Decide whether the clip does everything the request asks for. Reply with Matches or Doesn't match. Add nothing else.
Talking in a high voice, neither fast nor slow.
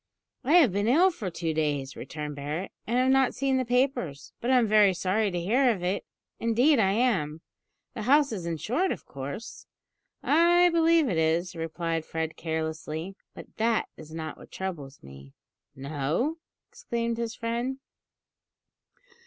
Matches